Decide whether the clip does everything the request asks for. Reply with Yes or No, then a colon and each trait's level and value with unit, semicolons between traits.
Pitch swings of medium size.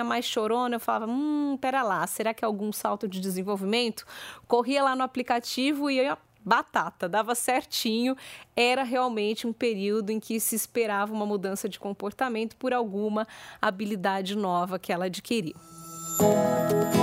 Yes: average, 3.2 semitones